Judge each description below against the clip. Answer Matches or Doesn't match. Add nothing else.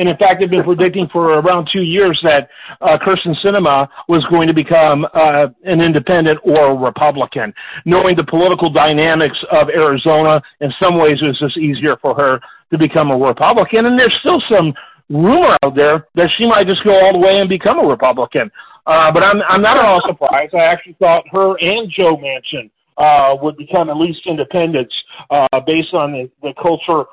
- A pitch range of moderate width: Matches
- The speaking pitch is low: Doesn't match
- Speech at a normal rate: Matches